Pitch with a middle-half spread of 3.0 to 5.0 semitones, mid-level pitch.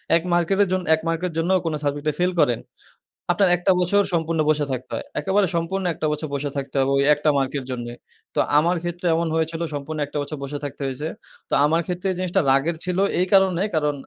Yes: average, 3.6 semitones; medium, 160 Hz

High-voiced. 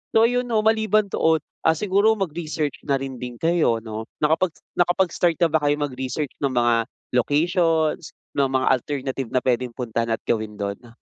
No: medium, 145 Hz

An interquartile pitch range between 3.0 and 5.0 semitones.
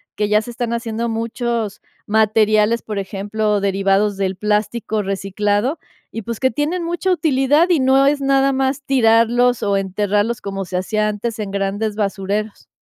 Yes: average, 3.3 semitones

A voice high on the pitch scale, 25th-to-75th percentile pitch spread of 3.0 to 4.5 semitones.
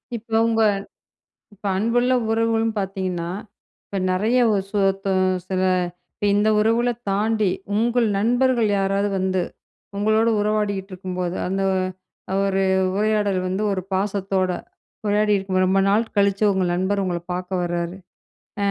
No: high, 200 Hz; narrow, 2.4 semitones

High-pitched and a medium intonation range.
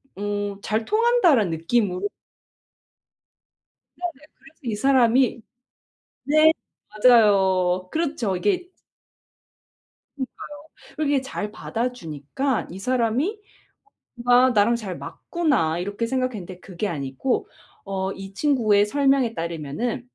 No: high, 230 Hz; wide, 5.8 semitones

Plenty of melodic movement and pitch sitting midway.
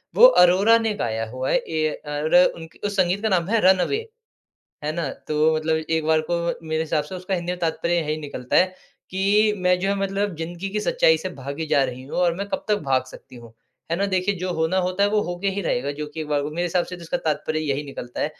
No: average, 3.7 semitones; medium, 170 Hz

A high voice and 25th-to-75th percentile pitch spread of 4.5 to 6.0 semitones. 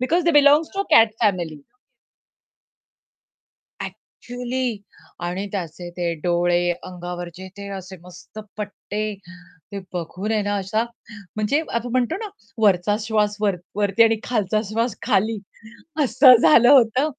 Yes: high, 210 Hz; average, 4.8 semitones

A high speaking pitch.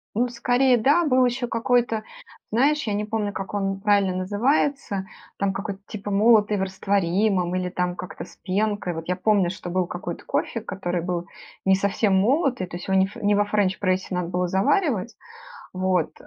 Yes: high, 200 Hz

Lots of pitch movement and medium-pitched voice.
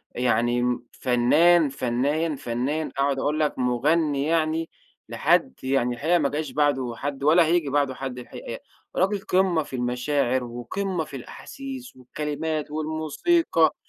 No: average, 4.1 semitones; medium, 145 Hz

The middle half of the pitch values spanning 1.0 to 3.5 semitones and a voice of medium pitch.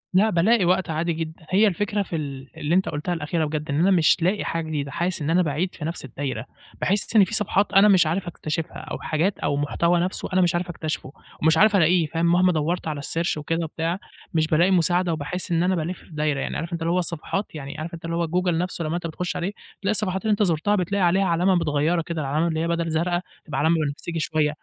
Yes: average, 2.7 semitones; medium, 170 Hz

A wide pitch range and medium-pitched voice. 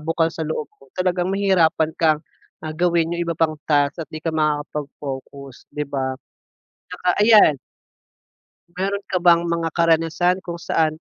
No: narrow, 2.4 semitones; medium, 165 Hz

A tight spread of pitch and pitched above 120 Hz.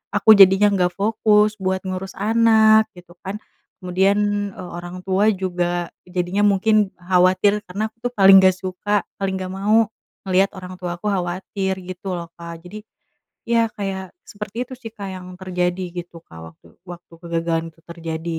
Yes: narrow, 2.3 semitones; medium, 185 Hz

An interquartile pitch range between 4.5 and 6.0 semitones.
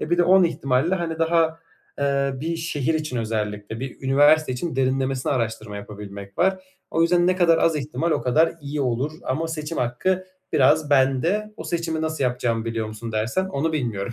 Yes: average, 5.1 semitones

